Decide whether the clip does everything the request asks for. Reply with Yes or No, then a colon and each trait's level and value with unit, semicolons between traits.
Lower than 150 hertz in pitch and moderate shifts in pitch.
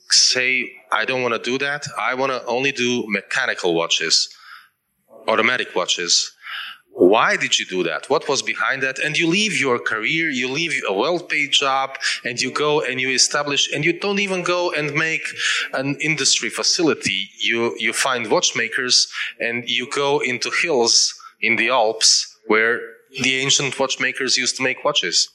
Yes: low, 135 Hz; average, 3.4 semitones